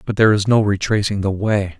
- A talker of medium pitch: No, low, 100 Hz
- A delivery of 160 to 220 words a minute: No, fast, 235 wpm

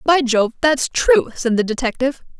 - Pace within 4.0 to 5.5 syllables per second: Yes, 4.9 syllables/s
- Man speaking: No, female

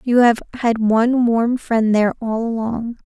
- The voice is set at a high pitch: Yes, high, 230 Hz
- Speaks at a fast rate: No, average, 175 wpm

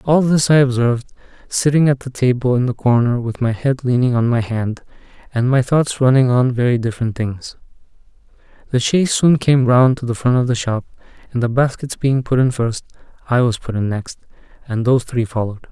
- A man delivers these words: Yes, male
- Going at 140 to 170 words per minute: No, average, 200 wpm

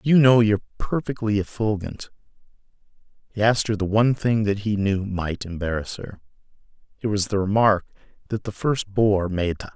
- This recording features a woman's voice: No, male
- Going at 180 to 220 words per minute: No, average, 170 wpm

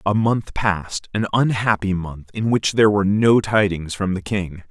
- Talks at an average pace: Yes, average, 190 wpm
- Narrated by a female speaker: No, male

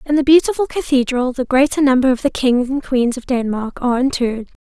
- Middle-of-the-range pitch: No, very high, 260 Hz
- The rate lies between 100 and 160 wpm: No, fast, 205 wpm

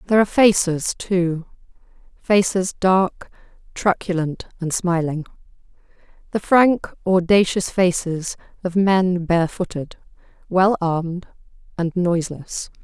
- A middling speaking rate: No, slow, 90 wpm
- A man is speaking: No, female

